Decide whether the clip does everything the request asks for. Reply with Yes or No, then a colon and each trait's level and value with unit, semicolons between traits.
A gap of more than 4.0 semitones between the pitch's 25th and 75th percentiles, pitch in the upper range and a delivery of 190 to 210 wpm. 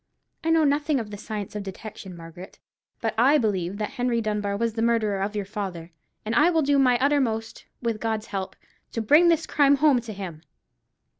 Yes: average, 5.3 semitones; high, 225 Hz; average, 200 wpm